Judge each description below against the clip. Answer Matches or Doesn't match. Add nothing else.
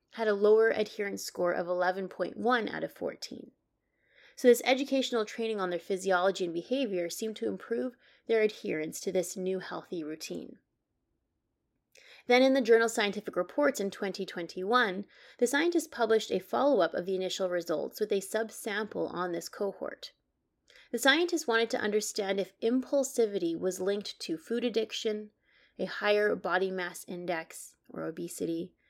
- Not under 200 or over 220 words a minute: Doesn't match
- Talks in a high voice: Matches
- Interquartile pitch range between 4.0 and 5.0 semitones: Matches